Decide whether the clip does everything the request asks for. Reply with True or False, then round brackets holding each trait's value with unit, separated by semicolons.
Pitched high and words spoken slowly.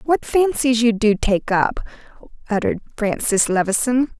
True (230 Hz; 130 wpm)